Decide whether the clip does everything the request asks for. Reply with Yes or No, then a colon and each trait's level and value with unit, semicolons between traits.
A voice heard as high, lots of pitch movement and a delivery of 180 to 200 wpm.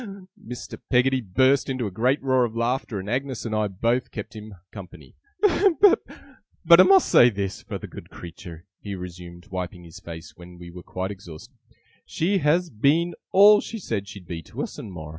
No: low, 110 Hz; wide, 6.8 semitones; average, 190 wpm